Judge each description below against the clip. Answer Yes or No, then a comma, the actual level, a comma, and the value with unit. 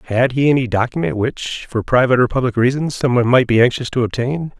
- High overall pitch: No, low, 125 Hz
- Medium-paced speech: No, fast, 210 wpm